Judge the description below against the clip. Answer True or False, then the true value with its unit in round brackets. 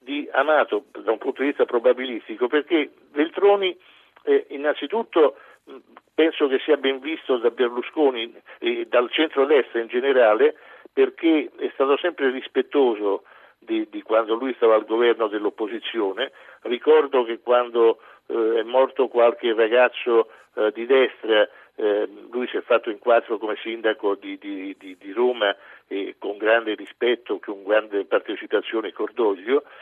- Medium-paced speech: True (140 wpm)